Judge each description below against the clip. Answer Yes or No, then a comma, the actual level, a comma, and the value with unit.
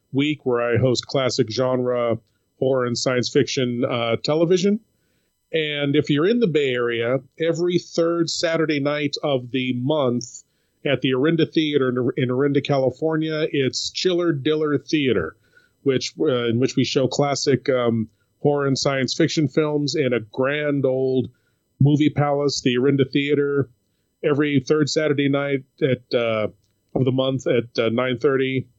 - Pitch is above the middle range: No, low, 135 Hz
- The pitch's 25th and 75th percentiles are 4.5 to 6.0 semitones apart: No, average, 3.2 semitones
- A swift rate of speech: No, average, 150 wpm